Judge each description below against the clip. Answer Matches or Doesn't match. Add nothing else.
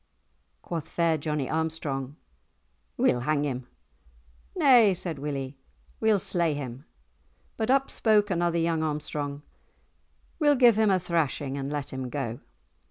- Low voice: Doesn't match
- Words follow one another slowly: Matches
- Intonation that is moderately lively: Matches